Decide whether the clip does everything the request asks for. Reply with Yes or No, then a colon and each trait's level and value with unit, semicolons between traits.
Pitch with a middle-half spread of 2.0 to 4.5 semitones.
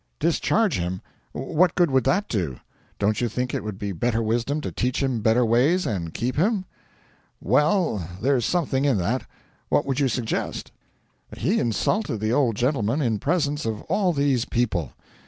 No: average, 5.0 semitones